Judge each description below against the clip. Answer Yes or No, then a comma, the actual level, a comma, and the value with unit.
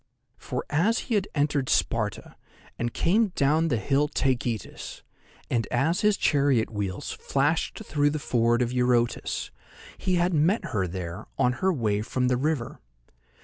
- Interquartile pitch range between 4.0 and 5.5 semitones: Yes, average, 5.2 semitones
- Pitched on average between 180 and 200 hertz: No, low, 135 Hz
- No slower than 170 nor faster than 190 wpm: No, average, 145 wpm